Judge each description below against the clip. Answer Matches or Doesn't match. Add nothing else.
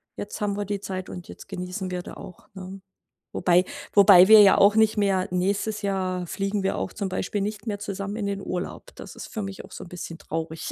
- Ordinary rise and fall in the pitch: Doesn't match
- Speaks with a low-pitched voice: Doesn't match